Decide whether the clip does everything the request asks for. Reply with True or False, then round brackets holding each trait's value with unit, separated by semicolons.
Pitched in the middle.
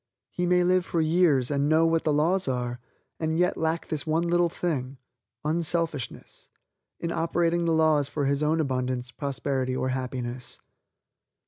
True (155 Hz)